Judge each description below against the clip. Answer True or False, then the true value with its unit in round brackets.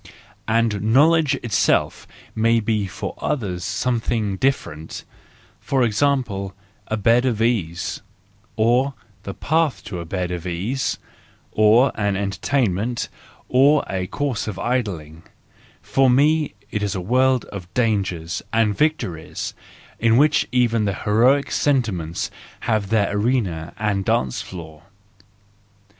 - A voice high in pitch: False (110 Hz)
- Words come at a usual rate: False (120 wpm)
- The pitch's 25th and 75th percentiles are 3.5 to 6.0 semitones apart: True (4.8 semitones)